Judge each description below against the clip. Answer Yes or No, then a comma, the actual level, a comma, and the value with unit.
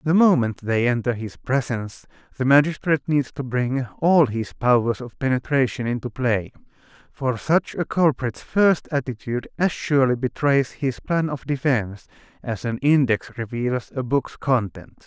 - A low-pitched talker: Yes, low, 130 Hz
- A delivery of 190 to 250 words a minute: No, average, 150 wpm